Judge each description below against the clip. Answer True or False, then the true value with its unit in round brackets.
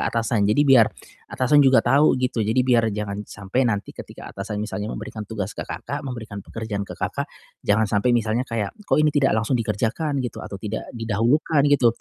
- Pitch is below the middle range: True (115 Hz)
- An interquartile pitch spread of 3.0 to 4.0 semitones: True (3.6 semitones)